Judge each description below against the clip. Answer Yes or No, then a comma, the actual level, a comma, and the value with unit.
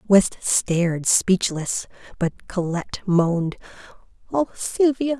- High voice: Yes, high, 195 Hz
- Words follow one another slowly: Yes, slow, 90 wpm